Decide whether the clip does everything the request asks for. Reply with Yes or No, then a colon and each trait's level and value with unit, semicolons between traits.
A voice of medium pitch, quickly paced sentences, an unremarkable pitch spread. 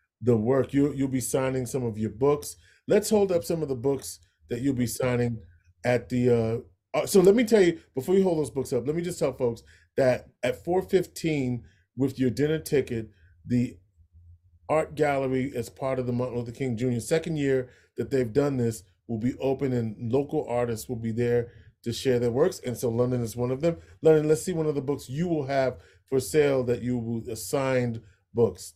No: low, 125 Hz; fast, 210 wpm; average, 3.6 semitones